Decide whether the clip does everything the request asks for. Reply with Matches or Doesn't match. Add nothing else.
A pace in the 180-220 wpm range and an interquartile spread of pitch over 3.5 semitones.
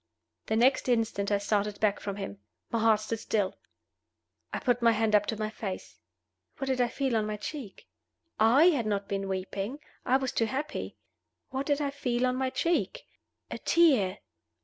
Matches